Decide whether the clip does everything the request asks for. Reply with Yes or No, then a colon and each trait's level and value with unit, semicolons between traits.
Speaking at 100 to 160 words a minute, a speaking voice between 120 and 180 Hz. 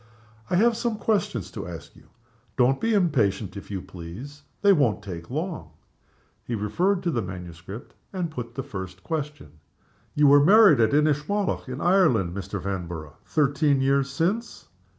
Yes: average, 155 wpm; low, 135 Hz